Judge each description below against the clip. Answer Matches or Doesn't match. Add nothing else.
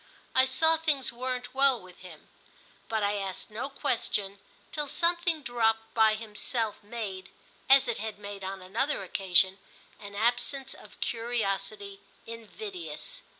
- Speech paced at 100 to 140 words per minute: Matches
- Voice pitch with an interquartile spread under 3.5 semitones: Doesn't match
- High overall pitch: Matches